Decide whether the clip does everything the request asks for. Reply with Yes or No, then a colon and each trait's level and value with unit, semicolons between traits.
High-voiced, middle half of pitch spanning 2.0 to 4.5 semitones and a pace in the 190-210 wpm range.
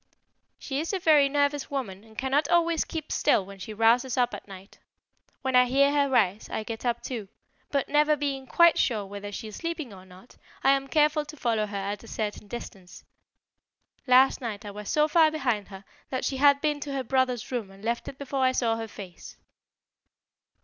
No: very high, 255 Hz; average, 5.2 semitones; fast, 205 wpm